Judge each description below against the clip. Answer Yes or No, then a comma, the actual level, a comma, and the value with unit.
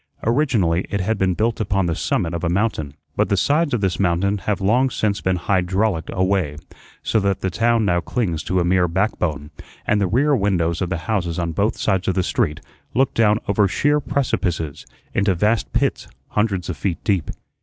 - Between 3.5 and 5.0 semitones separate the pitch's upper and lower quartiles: Yes, average, 3.8 semitones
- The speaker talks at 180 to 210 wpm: Yes, fast, 205 wpm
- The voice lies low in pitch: Yes, very low, 95 Hz